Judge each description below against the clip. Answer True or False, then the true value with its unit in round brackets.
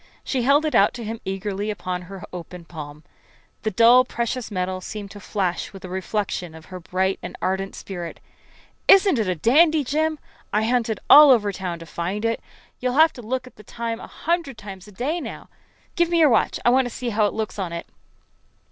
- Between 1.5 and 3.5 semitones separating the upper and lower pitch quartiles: False (5.3 semitones)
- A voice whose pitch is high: True (215 Hz)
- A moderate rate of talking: False (210 wpm)